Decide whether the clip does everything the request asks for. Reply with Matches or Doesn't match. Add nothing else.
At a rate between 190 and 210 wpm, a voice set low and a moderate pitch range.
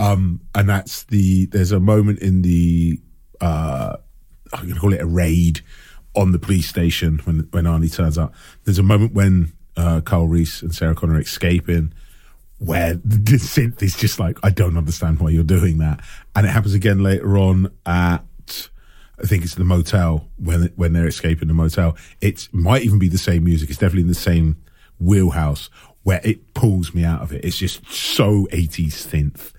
Matches